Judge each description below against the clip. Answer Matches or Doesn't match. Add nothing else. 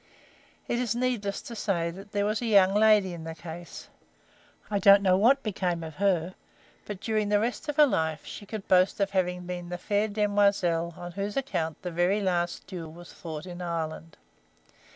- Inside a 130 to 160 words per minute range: Doesn't match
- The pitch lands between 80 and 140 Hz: Doesn't match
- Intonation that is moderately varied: Matches